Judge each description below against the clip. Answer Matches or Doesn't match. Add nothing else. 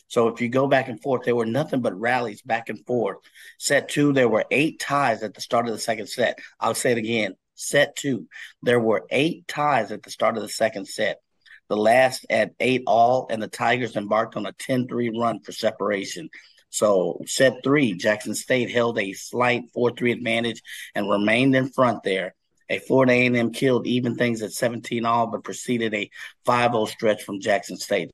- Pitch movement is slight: Matches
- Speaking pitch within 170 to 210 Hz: Doesn't match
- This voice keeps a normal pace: Matches